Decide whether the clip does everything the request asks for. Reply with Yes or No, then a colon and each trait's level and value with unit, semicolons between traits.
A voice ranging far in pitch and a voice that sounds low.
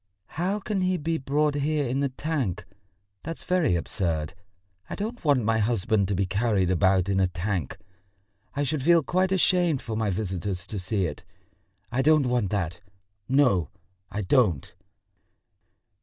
Yes: wide, 8.1 semitones; low, 115 Hz